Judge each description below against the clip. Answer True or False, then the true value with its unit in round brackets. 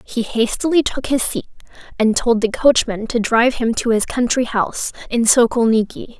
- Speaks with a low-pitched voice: False (235 Hz)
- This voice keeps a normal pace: True (175 wpm)